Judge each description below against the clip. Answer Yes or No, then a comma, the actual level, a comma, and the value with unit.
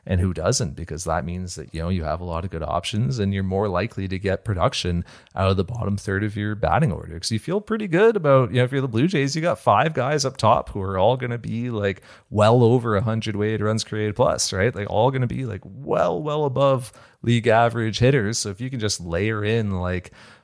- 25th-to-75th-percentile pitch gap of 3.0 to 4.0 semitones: No, average, 4.7 semitones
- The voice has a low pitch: Yes, low, 105 Hz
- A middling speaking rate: No, fast, 260 wpm